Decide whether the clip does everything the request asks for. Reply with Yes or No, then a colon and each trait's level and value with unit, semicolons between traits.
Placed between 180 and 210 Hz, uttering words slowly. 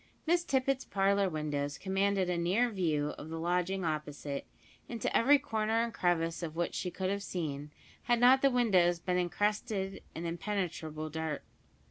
No: medium, 185 Hz; average, 160 wpm